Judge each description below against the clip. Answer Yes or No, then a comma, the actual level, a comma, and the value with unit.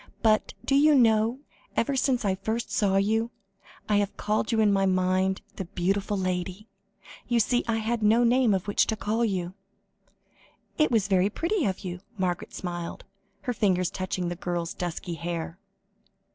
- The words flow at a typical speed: Yes, average, 170 wpm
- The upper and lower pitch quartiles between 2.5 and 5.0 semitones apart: Yes, average, 3.6 semitones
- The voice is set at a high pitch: Yes, high, 205 Hz